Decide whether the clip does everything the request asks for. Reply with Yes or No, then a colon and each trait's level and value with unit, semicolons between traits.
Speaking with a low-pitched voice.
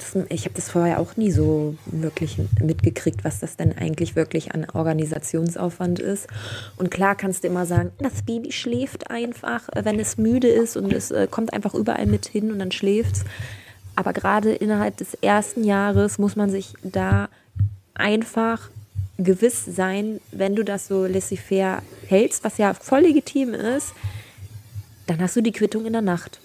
No: high, 190 Hz